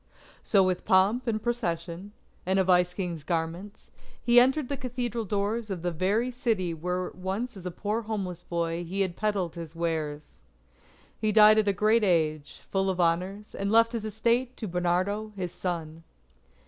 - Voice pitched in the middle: No, high, 195 Hz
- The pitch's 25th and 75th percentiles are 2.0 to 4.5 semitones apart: Yes, average, 3.9 semitones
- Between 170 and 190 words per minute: Yes, average, 175 wpm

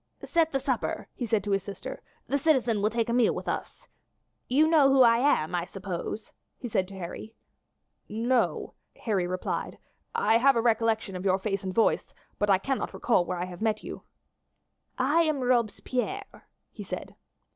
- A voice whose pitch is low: No, high, 225 Hz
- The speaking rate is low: No, average, 180 wpm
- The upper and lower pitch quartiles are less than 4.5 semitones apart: No, average, 4.9 semitones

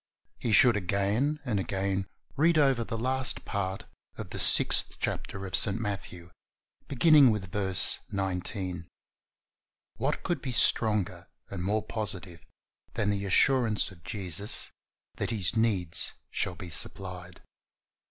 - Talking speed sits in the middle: No, slow, 130 wpm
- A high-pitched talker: No, low, 100 Hz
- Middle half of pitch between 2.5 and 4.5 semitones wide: Yes, average, 3.8 semitones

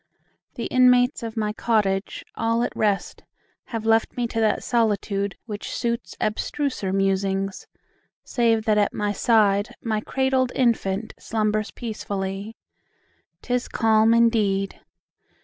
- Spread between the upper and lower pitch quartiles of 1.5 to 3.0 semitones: Yes, narrow, 2.6 semitones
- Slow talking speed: Yes, slow, 120 wpm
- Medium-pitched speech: No, high, 220 Hz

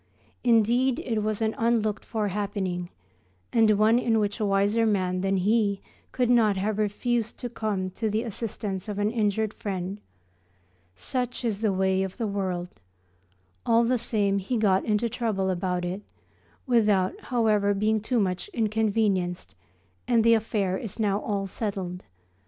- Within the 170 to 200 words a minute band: No, average, 155 wpm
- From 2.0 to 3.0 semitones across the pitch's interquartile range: Yes, average, 2.7 semitones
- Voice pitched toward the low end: No, high, 210 Hz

